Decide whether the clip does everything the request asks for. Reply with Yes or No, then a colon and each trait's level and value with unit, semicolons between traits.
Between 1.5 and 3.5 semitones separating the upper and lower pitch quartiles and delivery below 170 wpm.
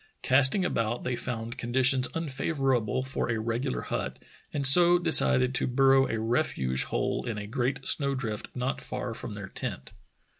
Yes: average, 3.0 semitones; average, 160 wpm